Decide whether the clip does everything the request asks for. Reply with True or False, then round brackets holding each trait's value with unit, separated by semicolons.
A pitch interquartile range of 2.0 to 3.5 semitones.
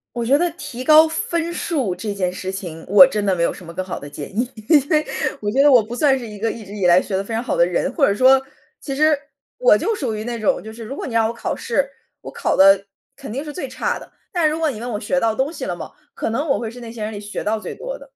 False (5.4 semitones)